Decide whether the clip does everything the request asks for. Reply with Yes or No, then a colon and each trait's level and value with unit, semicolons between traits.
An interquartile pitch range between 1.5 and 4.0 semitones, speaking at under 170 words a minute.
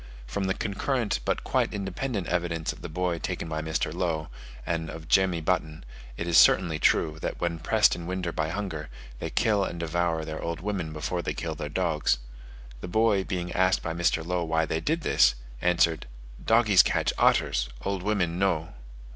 No: average, 2.9 semitones; average, 185 wpm